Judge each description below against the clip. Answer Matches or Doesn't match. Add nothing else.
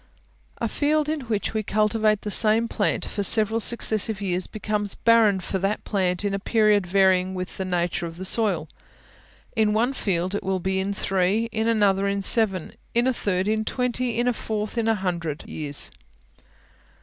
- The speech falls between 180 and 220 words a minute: Matches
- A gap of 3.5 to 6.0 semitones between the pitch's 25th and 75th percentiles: Doesn't match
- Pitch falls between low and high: Doesn't match